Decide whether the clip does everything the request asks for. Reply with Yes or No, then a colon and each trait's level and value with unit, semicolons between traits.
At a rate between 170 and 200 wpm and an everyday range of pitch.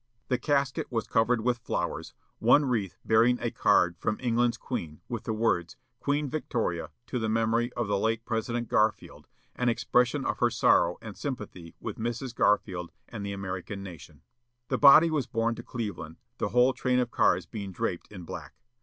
Yes: average, 180 wpm; average, 3.9 semitones